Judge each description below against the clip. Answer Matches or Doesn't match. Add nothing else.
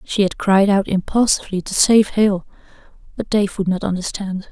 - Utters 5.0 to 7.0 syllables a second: Matches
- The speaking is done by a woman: Matches